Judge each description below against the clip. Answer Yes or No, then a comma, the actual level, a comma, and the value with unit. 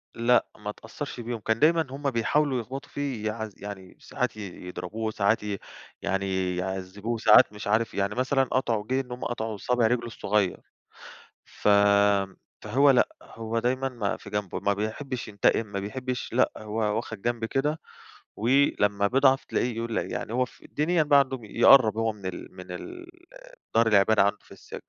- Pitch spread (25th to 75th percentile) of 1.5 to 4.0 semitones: Yes, average, 3.7 semitones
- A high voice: No, low, 115 Hz